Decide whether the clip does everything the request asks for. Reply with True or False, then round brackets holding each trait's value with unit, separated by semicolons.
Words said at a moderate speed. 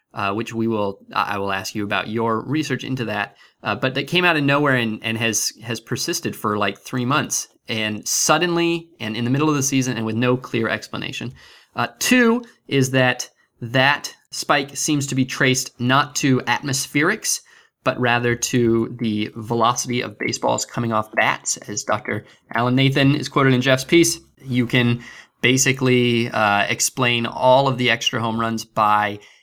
True (175 wpm)